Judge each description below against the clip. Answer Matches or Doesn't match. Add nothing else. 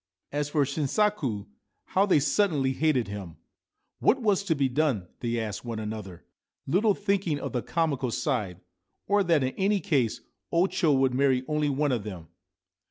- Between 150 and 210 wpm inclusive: Matches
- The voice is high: Doesn't match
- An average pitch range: Doesn't match